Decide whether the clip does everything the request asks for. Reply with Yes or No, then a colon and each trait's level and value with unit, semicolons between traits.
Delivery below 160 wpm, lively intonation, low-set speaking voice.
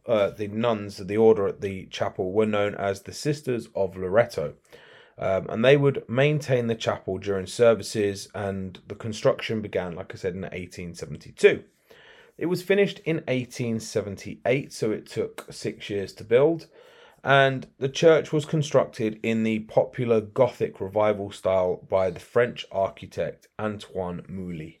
Yes: average, 150 wpm; wide, 5.7 semitones; low, 110 Hz